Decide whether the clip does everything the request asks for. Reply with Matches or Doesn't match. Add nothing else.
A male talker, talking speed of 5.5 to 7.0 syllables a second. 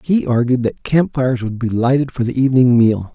Matches